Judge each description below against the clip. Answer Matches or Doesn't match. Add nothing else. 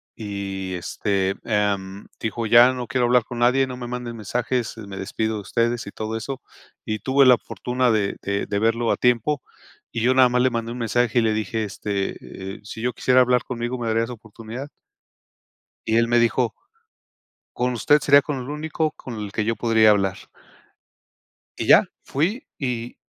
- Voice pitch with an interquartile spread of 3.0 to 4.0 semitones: Doesn't match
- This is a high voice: Doesn't match